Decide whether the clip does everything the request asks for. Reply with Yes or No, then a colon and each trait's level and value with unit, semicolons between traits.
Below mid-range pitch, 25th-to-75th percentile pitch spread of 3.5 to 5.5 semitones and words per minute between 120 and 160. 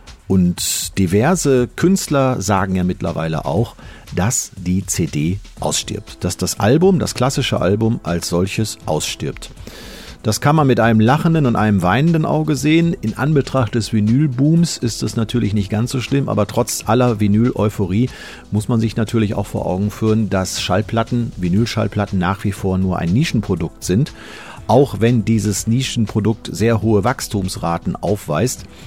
Yes: low, 110 Hz; average, 4.3 semitones; average, 150 wpm